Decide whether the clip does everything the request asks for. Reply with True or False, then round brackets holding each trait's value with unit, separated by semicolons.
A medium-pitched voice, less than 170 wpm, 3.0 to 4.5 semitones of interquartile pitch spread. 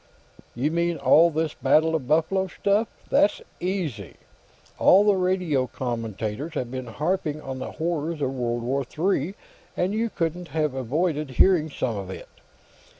False (155 Hz; 150 wpm; 5.2 semitones)